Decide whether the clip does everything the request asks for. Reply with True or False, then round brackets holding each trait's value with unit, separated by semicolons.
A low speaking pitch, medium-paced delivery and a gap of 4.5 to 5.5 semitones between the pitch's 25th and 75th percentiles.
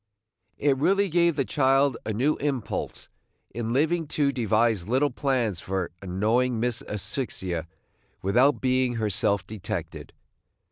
False (125 Hz; 125 wpm; 4.8 semitones)